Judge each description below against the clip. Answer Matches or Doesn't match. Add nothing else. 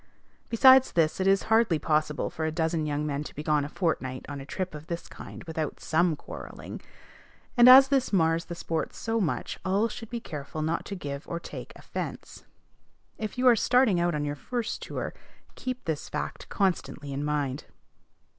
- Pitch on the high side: Doesn't match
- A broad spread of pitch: Matches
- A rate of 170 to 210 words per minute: Matches